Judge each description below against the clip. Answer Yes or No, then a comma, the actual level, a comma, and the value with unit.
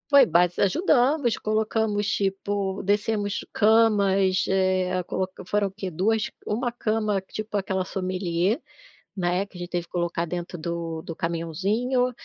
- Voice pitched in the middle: No, high, 195 Hz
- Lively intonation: No, average, 3.1 semitones